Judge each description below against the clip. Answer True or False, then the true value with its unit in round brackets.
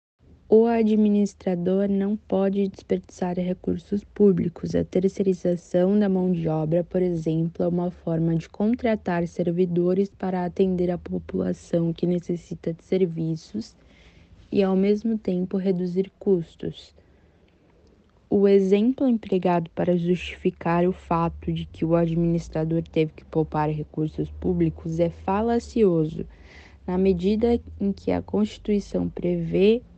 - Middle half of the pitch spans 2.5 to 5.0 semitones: True (3.0 semitones)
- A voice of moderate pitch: True (180 Hz)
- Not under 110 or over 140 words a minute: True (120 wpm)